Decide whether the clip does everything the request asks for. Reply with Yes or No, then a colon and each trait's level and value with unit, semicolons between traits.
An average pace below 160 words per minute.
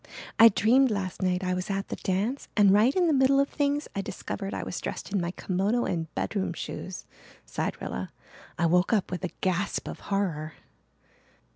No: average, 190 wpm